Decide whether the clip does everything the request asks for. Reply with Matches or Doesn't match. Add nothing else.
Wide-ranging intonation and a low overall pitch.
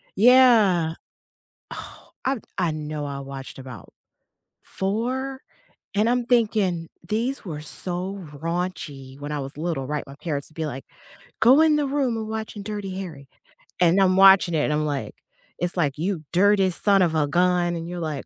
Doesn't match